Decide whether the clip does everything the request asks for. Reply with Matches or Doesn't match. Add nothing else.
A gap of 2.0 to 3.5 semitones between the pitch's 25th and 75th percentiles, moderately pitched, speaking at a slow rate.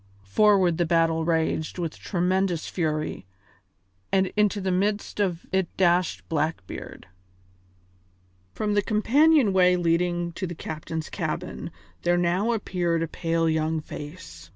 Matches